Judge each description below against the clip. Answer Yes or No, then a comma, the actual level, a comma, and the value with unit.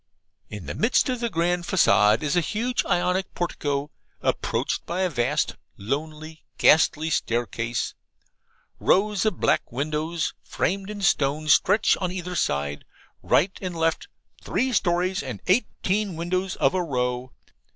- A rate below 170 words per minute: Yes, average, 140 wpm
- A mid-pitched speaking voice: Yes, medium, 170 Hz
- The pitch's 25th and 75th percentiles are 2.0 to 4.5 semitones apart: No, average, 5.0 semitones